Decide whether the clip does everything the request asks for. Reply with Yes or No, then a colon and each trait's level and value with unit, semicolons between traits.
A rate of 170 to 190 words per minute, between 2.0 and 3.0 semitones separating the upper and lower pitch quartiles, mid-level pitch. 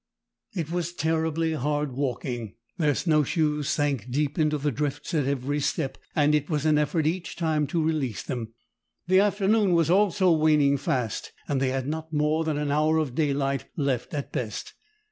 Yes: average, 180 wpm; narrow, 2.5 semitones; medium, 150 Hz